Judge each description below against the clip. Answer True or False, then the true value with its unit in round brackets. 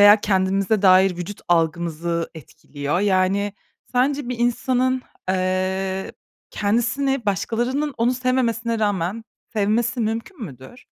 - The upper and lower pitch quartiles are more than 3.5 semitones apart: True (4.5 semitones)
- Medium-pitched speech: False (205 Hz)